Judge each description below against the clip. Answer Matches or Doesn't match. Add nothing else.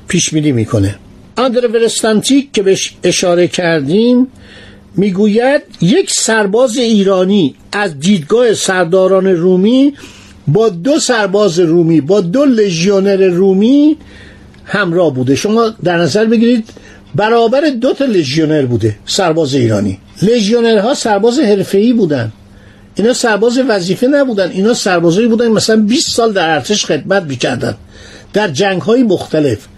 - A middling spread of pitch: Doesn't match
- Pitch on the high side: Matches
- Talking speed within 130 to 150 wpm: Doesn't match